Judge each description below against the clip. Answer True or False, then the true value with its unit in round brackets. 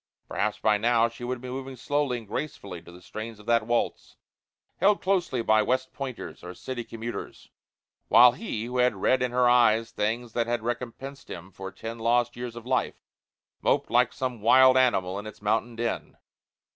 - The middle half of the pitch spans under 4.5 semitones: True (2.6 semitones)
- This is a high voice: False (120 Hz)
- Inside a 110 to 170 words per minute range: False (185 wpm)